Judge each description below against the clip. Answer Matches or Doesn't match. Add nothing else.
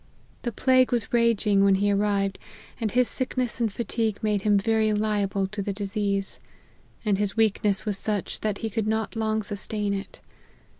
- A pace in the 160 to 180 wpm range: Matches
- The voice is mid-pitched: Doesn't match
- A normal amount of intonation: Doesn't match